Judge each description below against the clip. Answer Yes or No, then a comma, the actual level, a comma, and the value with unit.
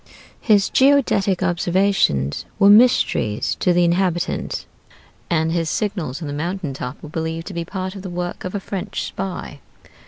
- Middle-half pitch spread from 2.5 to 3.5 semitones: Yes, average, 3.2 semitones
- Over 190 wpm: No, average, 160 wpm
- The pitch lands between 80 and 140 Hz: No, medium, 175 Hz